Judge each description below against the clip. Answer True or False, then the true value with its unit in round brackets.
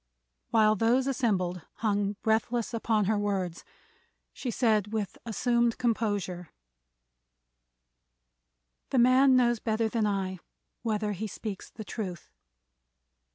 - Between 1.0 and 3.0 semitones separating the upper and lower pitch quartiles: True (2.7 semitones)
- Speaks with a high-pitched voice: True (220 Hz)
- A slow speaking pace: True (110 wpm)